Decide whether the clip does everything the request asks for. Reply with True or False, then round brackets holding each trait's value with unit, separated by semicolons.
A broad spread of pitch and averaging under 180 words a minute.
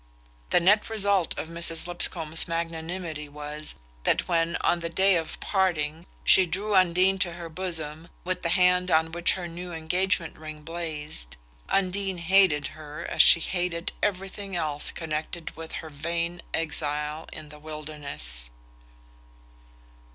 False (2.7 semitones; 140 wpm)